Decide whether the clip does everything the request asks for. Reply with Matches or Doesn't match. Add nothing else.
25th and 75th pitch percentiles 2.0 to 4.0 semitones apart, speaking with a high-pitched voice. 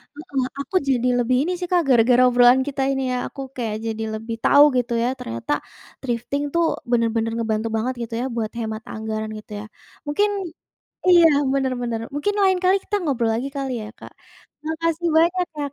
Doesn't match